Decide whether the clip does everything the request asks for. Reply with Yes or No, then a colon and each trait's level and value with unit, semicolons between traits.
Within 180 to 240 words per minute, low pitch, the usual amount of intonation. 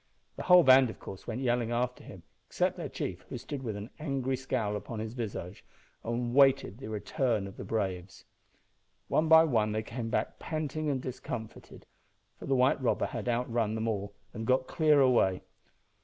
Yes: average, 185 wpm; low, 120 Hz; average, 3.5 semitones